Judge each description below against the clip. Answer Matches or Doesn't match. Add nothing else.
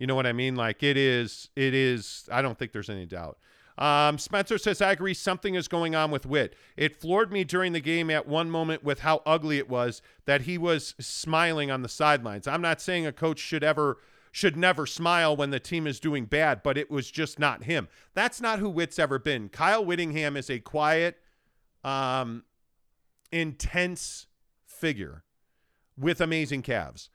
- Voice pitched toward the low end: Doesn't match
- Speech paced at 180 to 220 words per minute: Matches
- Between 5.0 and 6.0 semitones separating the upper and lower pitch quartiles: Doesn't match